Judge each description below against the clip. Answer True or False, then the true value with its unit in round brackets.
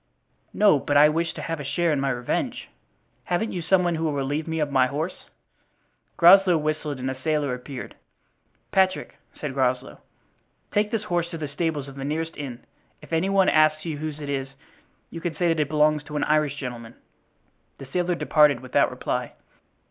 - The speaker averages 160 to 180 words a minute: False (195 wpm)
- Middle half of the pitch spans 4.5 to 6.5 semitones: False (3.3 semitones)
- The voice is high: False (155 Hz)